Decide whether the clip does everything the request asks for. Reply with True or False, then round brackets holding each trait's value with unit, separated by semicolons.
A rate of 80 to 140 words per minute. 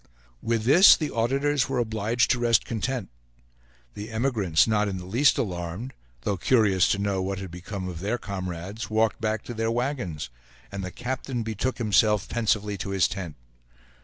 False (170 wpm)